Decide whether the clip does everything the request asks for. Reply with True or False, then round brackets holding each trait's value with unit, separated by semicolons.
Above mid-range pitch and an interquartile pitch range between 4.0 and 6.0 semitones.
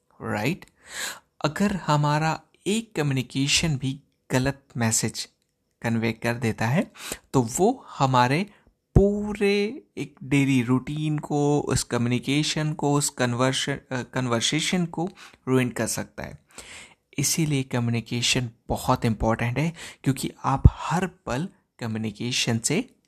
False (135 Hz; 4.4 semitones)